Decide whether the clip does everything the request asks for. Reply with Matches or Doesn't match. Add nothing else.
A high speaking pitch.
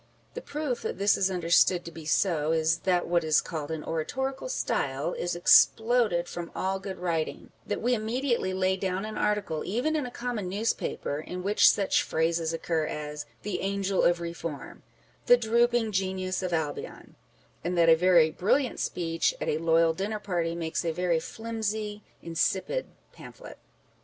Doesn't match